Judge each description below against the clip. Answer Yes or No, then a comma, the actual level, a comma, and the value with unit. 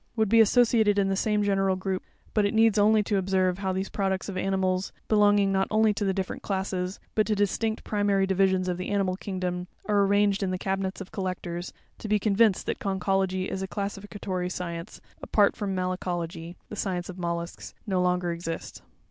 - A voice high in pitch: Yes, high, 195 Hz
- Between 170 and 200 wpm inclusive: Yes, average, 190 wpm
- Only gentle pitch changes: Yes, narrow, 1.9 semitones